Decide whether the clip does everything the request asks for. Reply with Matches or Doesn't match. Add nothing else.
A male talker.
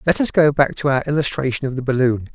Matches